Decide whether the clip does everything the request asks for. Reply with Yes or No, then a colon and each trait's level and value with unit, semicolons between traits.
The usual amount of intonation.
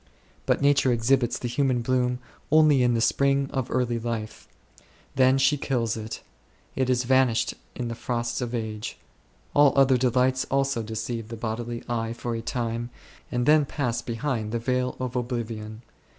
No: narrow, 2.2 semitones